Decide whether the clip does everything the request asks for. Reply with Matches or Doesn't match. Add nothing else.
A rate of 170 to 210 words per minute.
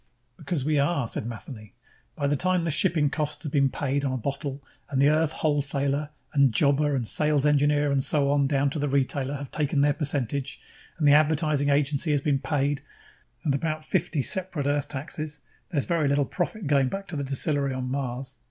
Matches